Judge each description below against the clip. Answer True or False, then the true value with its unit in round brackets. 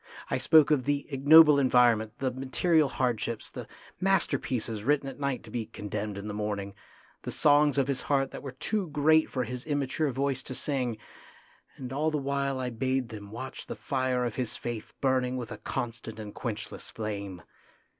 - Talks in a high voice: False (130 Hz)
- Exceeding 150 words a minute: True (185 wpm)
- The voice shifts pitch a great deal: False (3.6 semitones)